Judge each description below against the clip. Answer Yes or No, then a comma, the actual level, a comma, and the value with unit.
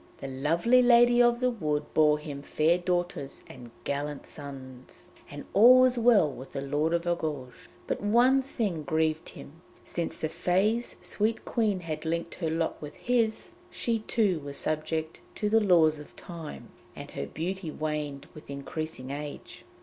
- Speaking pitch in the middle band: Yes, medium, 160 Hz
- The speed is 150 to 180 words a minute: Yes, average, 165 wpm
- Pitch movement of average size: No, wide, 6.2 semitones